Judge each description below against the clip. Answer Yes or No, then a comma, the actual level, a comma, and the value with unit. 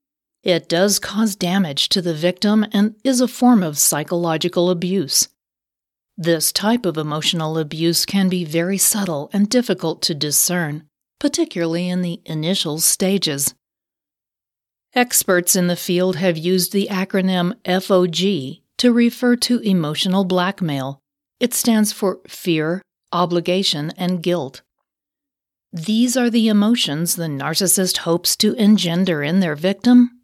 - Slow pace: Yes, slow, 130 wpm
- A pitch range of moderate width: Yes, average, 3.9 semitones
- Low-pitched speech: No, medium, 180 Hz